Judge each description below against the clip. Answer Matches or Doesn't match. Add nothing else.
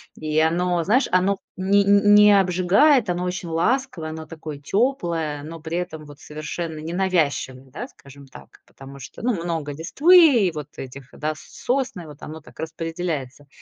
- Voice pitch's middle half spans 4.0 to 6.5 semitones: Matches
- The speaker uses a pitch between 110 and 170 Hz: Matches